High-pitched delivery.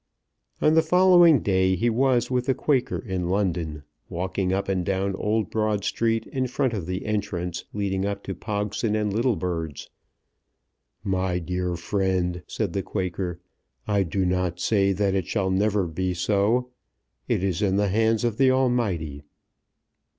No: low, 100 Hz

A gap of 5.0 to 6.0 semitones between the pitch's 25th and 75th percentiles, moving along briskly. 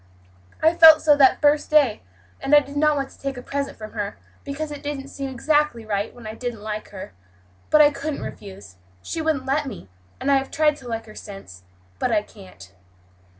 Yes: wide, 5.5 semitones; fast, 215 wpm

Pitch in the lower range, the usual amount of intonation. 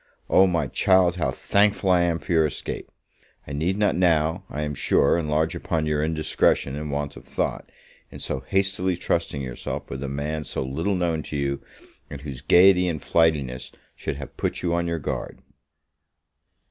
Yes: very low, 80 Hz; average, 3.5 semitones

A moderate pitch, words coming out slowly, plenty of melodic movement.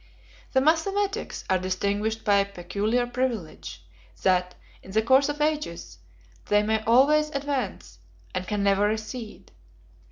No: high, 220 Hz; slow, 130 wpm; wide, 5.8 semitones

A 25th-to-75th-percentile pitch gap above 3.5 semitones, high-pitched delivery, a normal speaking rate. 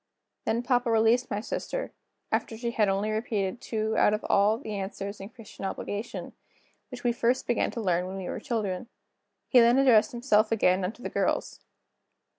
No: average, 3.0 semitones; high, 220 Hz; average, 180 wpm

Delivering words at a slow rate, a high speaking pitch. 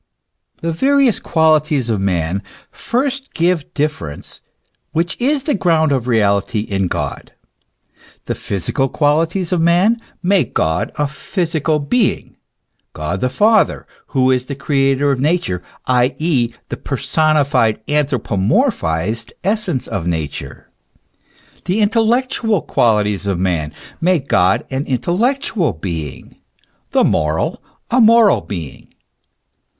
No: slow, 120 wpm; medium, 145 Hz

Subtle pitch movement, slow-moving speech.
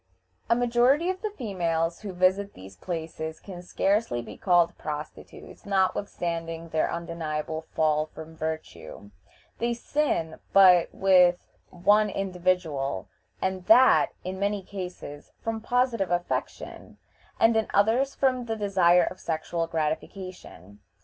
No: average, 4.3 semitones; slow, 125 wpm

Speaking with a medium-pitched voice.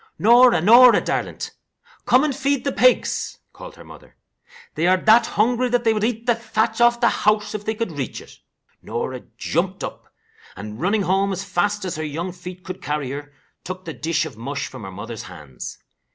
No: high, 200 Hz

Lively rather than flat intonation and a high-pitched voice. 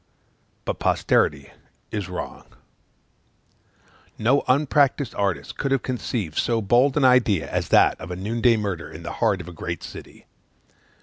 No: wide, 5.9 semitones; low, 110 Hz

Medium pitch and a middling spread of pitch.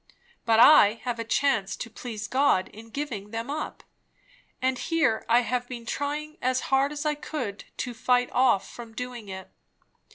No: high, 245 Hz; average, 3.7 semitones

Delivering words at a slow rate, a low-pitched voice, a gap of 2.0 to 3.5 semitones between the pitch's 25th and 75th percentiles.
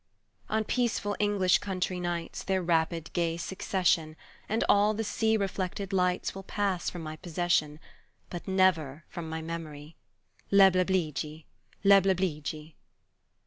No: slow, 120 wpm; medium, 180 Hz; average, 3.2 semitones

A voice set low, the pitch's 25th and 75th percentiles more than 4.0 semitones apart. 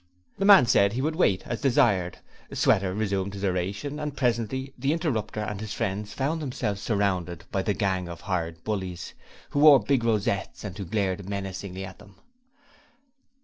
Yes: low, 100 Hz; average, 4.6 semitones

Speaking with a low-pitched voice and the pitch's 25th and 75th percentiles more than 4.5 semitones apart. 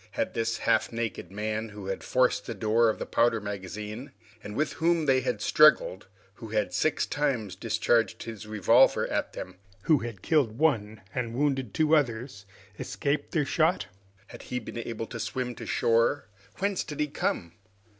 Yes: low, 115 Hz; average, 4.9 semitones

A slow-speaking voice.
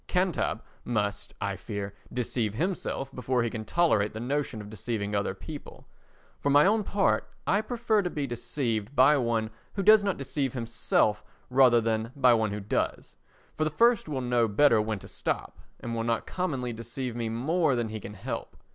No: average, 185 wpm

